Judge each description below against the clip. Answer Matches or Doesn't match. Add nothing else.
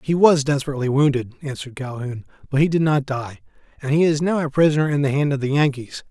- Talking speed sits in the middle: Doesn't match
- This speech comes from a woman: Doesn't match